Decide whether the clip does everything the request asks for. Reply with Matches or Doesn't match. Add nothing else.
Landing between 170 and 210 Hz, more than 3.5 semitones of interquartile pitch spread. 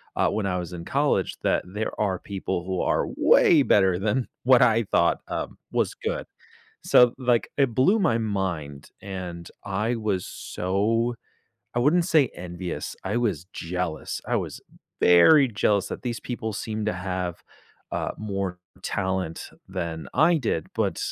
Doesn't match